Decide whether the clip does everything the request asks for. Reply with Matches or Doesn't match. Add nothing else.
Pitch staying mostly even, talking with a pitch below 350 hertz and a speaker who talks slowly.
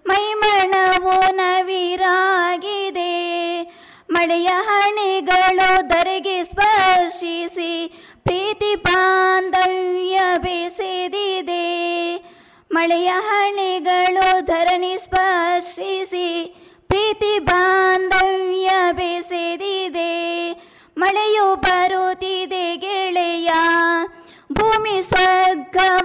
Doesn't match